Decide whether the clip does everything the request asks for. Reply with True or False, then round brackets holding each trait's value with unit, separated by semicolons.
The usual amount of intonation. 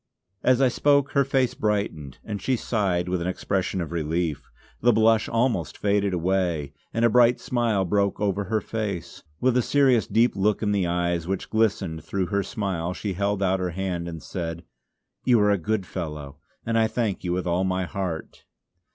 True (4.2 semitones)